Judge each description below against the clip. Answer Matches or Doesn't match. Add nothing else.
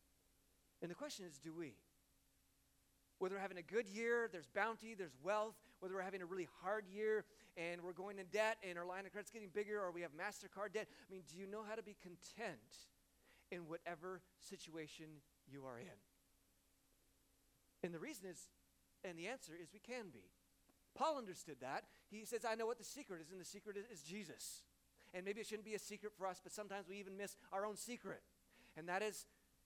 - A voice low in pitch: Doesn't match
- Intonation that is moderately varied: Matches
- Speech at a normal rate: Doesn't match